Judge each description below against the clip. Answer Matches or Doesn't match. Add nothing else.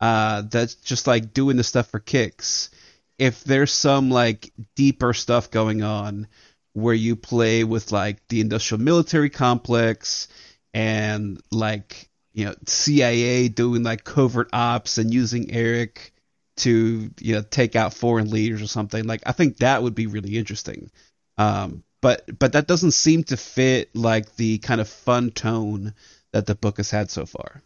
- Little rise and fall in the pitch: Matches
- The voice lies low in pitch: Matches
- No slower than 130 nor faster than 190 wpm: Matches